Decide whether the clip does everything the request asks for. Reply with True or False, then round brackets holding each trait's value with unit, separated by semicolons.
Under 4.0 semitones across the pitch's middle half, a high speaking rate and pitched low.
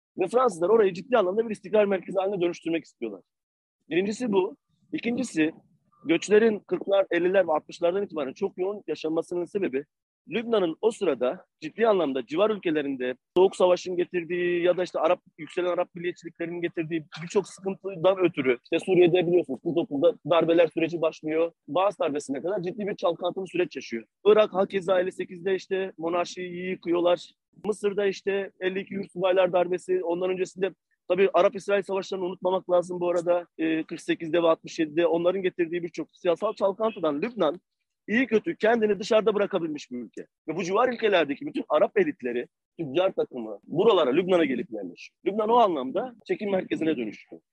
False (2.8 semitones; 150 wpm; 180 Hz)